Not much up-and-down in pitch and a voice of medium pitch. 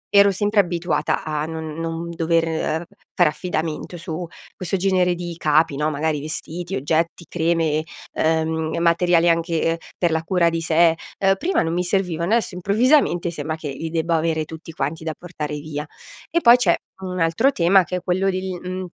Yes: narrow, 2.2 semitones; medium, 165 Hz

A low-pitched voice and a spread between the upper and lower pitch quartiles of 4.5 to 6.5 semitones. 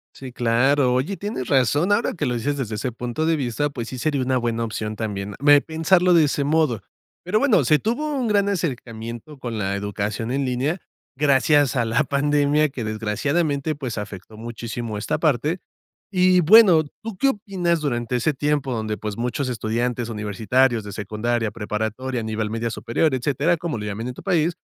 Yes: low, 130 Hz; average, 5.3 semitones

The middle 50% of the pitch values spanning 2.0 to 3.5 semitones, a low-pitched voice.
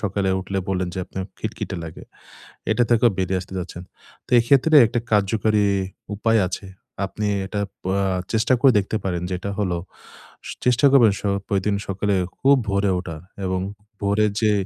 Yes: average, 2.8 semitones; low, 100 Hz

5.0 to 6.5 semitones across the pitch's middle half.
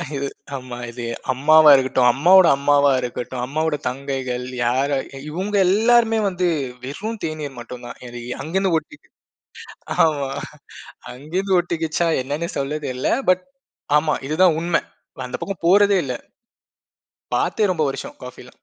Yes: wide, 5.4 semitones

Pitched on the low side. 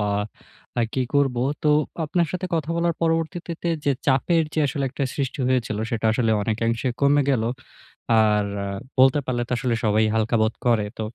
Yes: low, 130 Hz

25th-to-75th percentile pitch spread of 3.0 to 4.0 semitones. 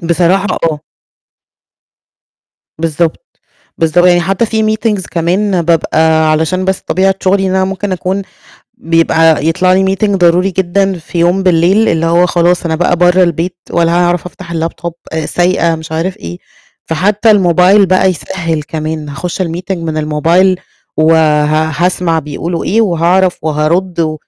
No: narrow, 2.6 semitones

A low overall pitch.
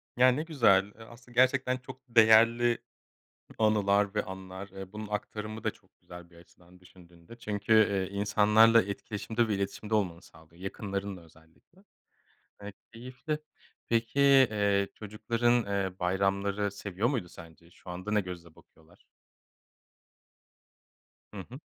Yes: low, 105 Hz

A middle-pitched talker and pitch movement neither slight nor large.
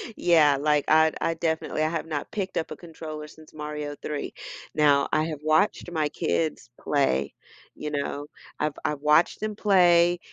No: medium, 155 Hz; narrow, 1.8 semitones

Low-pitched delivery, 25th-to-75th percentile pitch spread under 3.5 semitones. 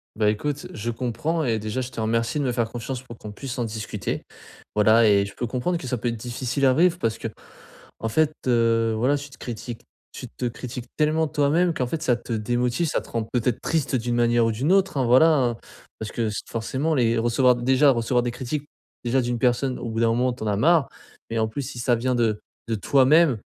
Yes: low, 120 Hz; average, 3.0 semitones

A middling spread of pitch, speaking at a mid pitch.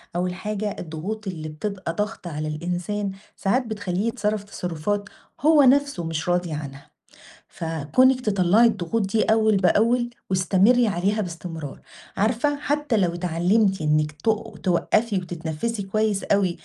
No: average, 4.2 semitones; high, 195 Hz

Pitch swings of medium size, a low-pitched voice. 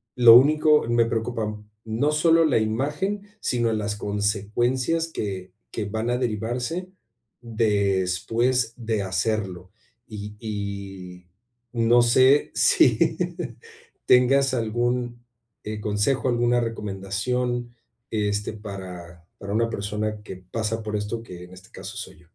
Yes: average, 3.1 semitones; low, 110 Hz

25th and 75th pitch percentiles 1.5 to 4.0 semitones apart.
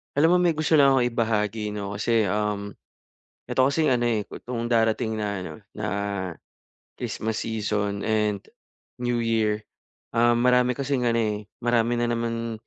Yes: narrow, 2.4 semitones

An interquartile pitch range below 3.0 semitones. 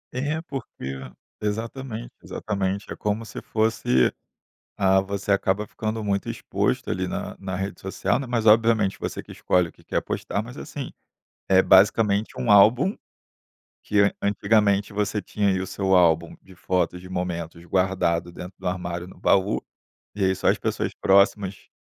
Yes: narrow, 2.6 semitones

